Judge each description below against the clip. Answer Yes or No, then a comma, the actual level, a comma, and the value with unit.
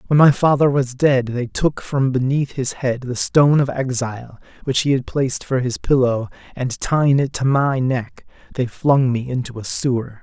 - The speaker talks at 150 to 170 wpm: No, average, 200 wpm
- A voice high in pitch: No, low, 130 Hz